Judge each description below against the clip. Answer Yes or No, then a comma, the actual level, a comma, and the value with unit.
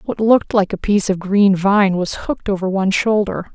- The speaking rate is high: Yes, fast, 220 wpm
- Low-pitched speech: No, high, 200 Hz